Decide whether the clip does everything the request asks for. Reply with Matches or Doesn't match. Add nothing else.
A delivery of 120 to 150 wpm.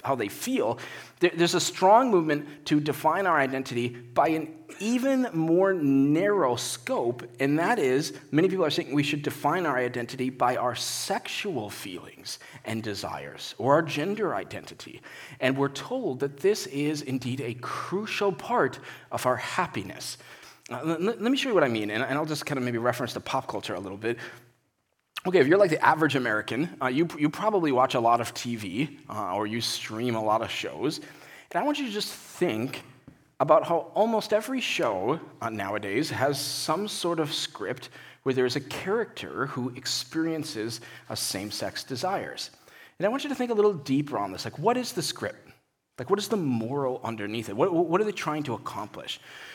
Doesn't match